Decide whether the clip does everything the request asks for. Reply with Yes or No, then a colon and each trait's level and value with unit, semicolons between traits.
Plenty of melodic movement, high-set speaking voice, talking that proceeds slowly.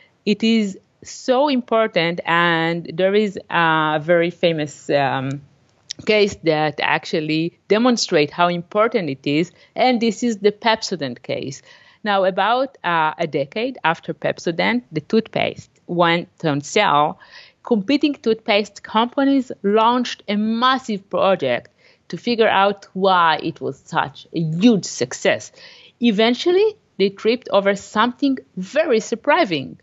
Yes: wide, 5.7 semitones; high, 200 Hz; slow, 125 wpm